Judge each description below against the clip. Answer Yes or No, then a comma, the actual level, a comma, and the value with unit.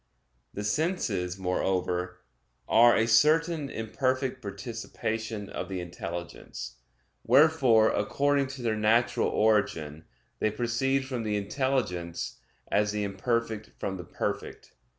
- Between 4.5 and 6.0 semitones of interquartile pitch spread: Yes, average, 5.2 semitones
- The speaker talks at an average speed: No, slow, 110 wpm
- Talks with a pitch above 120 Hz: No, low, 110 Hz